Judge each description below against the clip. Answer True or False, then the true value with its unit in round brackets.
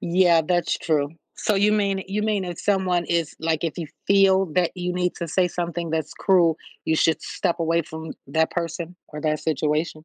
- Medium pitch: True (170 Hz)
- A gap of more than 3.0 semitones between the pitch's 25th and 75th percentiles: False (2.7 semitones)